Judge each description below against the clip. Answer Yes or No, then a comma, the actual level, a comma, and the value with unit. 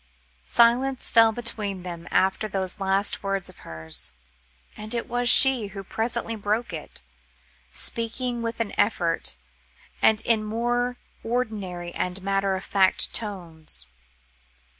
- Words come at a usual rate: No, slow, 125 wpm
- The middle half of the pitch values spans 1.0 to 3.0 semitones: No, average, 3.6 semitones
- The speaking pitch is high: Yes, high, 210 Hz